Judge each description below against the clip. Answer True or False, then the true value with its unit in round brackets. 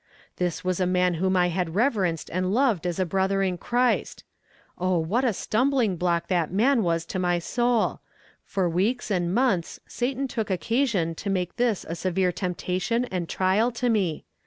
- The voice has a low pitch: False (185 Hz)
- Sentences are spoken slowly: False (180 wpm)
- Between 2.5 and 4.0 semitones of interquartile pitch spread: False (4.6 semitones)